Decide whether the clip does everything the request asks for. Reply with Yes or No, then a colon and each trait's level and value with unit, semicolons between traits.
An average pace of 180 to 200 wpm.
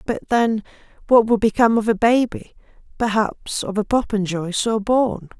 No: slow, 135 wpm